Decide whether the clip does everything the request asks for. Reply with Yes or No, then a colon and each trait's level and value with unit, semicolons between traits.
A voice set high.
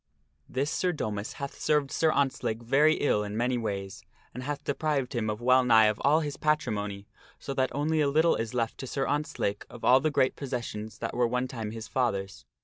No: low, 125 Hz